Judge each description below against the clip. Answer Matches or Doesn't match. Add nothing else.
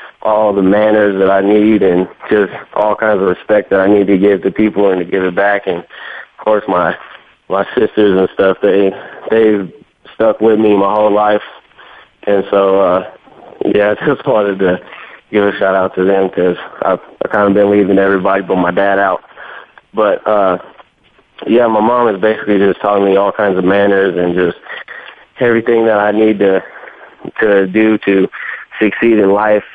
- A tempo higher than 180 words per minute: Matches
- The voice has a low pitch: Matches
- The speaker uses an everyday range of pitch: Doesn't match